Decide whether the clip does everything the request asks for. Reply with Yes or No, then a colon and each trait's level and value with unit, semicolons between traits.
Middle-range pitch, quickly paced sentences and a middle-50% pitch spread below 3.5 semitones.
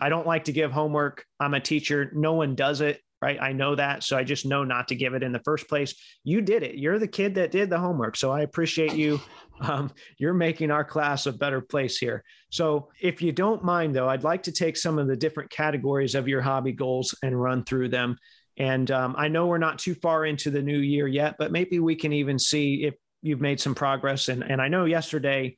Yes: medium, 145 Hz; fast, 245 wpm; average, 2.8 semitones